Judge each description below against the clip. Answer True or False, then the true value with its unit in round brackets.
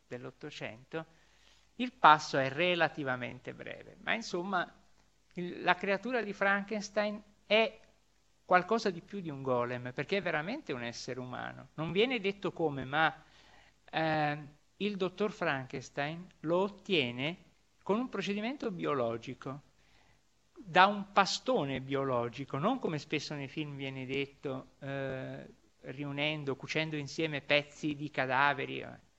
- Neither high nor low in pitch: True (155 Hz)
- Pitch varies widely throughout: True (6.3 semitones)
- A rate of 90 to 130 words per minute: True (120 wpm)